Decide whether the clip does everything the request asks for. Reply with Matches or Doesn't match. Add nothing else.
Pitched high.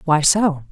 Doesn't match